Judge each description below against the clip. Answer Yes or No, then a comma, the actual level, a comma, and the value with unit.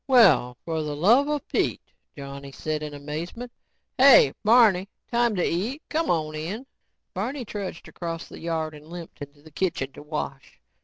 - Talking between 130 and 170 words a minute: Yes, average, 155 wpm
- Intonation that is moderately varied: No, wide, 7.2 semitones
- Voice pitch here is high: No, medium, 170 Hz